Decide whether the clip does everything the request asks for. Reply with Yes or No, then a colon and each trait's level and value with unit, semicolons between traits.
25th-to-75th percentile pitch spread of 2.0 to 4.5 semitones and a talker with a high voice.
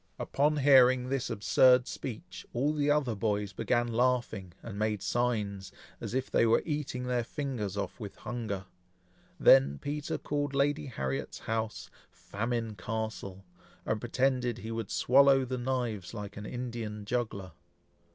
No: average, 3.7 semitones; low, 120 Hz